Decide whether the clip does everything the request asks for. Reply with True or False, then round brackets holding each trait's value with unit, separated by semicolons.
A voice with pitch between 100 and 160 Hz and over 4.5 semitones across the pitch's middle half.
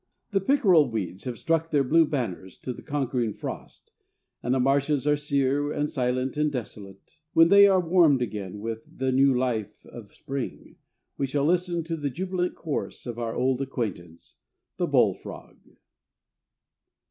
True (135 Hz; 4.9 semitones)